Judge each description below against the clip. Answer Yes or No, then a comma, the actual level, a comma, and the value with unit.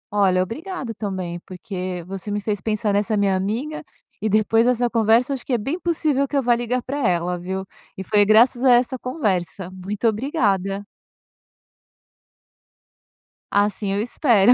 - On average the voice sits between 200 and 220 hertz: Yes, high, 215 Hz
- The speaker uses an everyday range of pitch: Yes, average, 4.3 semitones